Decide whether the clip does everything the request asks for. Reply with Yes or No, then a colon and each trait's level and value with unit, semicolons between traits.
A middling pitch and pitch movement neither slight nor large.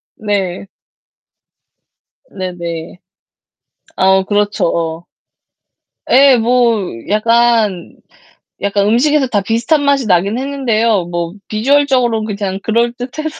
No: high, 220 Hz; average, 4.4 semitones